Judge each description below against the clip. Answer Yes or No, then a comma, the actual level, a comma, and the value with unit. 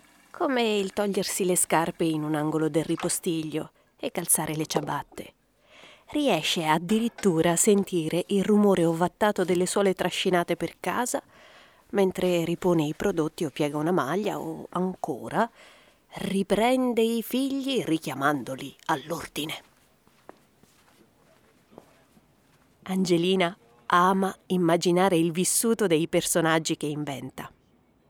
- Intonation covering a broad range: No, average, 3.7 semitones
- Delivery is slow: Yes, slow, 105 wpm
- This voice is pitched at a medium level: Yes, medium, 180 Hz